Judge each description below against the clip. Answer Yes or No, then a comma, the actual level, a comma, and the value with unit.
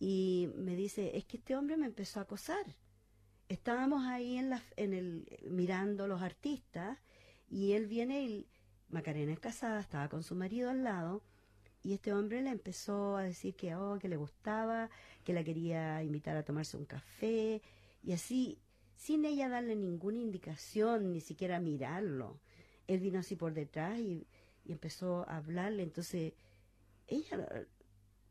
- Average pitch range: No, wide, 5.7 semitones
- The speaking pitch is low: No, medium, 185 Hz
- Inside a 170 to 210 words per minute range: No, average, 160 wpm